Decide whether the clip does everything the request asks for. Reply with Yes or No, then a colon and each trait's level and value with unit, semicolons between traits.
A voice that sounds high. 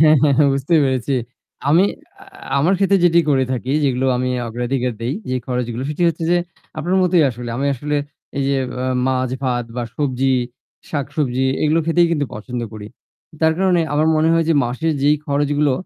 No: medium, 140 Hz